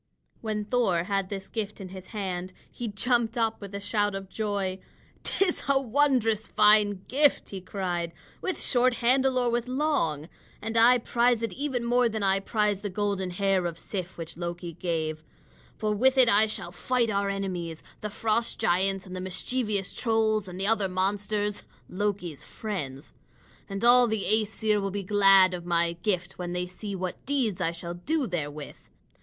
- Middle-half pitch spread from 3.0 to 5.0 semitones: Yes, average, 3.7 semitones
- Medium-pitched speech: No, high, 205 Hz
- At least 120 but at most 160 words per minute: No, average, 175 wpm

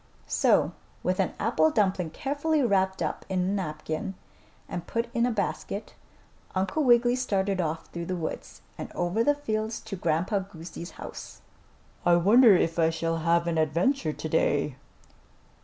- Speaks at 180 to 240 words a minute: No, average, 155 wpm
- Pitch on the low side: No, high, 190 Hz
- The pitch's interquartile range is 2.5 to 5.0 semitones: No, wide, 5.4 semitones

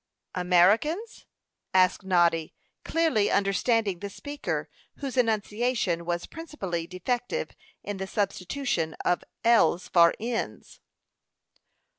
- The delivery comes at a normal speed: No, slow, 95 wpm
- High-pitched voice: Yes, high, 200 Hz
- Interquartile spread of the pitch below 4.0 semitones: No, wide, 5.6 semitones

